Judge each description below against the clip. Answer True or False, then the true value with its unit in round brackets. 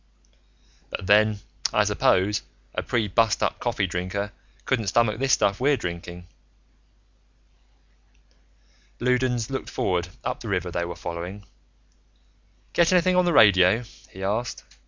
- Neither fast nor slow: False (125 wpm)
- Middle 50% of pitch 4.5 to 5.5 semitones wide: True (5.1 semitones)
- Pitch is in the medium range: False (105 Hz)